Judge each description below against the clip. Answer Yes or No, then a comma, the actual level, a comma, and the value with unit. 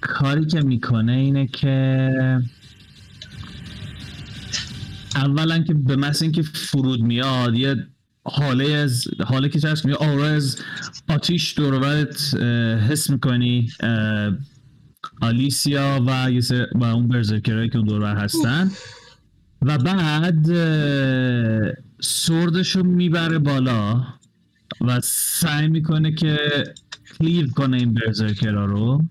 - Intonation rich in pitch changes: No, average, 3.9 semitones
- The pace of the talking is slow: Yes, slow, 100 wpm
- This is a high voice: No, low, 135 Hz